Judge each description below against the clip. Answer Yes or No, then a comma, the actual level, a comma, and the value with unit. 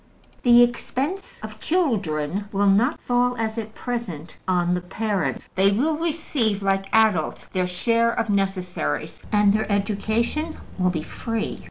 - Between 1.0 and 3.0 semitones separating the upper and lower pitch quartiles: No, average, 4.0 semitones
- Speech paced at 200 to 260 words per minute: No, average, 145 wpm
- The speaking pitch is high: Yes, high, 215 Hz